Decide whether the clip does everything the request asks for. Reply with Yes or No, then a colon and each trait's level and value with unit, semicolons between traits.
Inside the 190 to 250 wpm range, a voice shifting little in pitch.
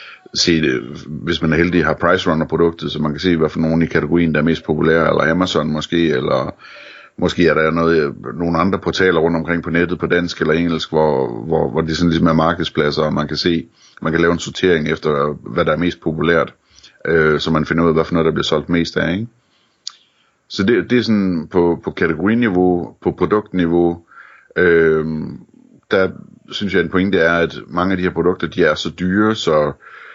Yes: average, 215 wpm; narrow, 1.5 semitones